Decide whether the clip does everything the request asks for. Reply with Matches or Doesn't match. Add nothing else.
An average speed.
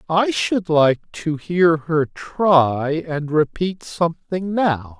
Doesn't match